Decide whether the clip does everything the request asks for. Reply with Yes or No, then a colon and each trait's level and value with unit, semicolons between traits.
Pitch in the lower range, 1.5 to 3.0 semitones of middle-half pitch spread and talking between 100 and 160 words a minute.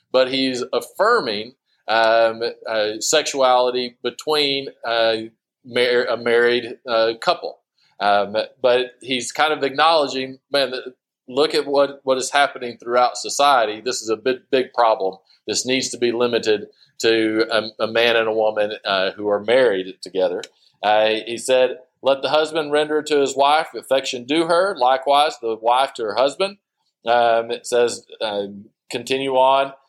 No: low, 125 Hz; average, 3.4 semitones; average, 155 wpm